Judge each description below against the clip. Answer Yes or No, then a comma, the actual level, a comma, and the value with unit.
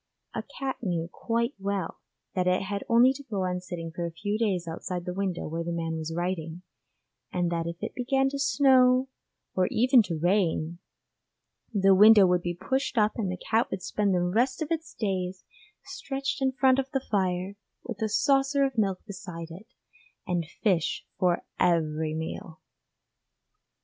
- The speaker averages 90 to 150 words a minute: No, average, 175 wpm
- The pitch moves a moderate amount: No, wide, 5.7 semitones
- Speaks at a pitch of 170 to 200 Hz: Yes, high, 190 Hz